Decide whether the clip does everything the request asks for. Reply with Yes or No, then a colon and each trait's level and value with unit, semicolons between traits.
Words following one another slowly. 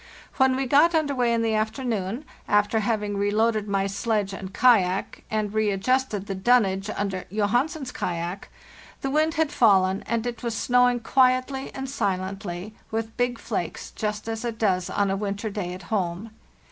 No: average, 160 wpm